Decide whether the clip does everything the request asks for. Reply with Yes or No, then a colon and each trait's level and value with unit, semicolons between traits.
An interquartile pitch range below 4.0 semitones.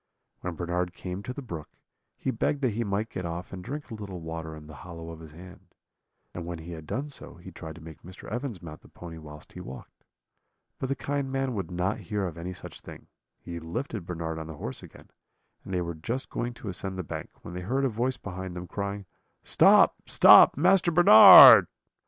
No: average, 5.3 semitones